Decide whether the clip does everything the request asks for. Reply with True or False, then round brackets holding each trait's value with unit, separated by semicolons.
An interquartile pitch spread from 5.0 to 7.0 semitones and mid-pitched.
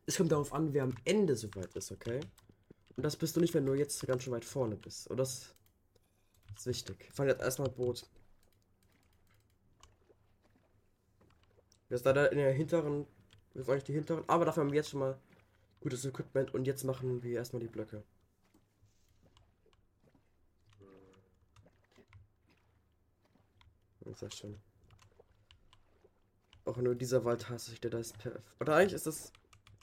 False (5.5 semitones; 105 Hz)